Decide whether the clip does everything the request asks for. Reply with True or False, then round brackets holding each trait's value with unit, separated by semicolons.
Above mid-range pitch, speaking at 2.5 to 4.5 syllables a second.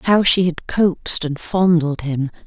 False (165 Hz; 4.4 syllables/s)